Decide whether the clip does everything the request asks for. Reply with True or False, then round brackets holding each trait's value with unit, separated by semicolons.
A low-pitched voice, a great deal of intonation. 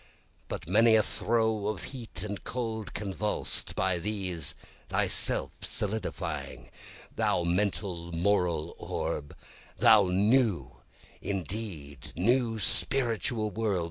False (105 Hz; 3.7 semitones)